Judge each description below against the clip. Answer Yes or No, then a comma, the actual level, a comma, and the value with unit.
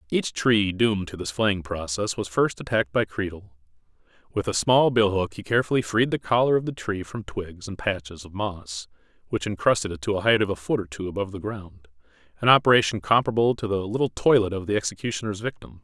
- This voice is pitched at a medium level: No, low, 105 Hz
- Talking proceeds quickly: Yes, fast, 210 wpm